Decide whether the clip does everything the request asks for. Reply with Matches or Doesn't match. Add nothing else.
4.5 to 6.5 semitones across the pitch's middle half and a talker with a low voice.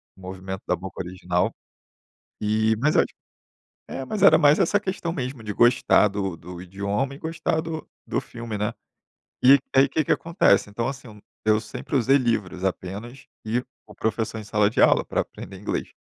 Matches